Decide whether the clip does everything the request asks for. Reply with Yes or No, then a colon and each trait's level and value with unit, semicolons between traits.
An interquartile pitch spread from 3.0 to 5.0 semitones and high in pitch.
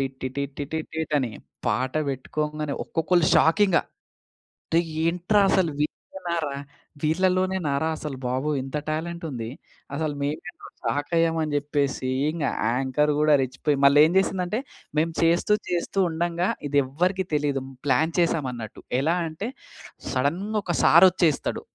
No: average, 3.3 semitones; medium, 155 Hz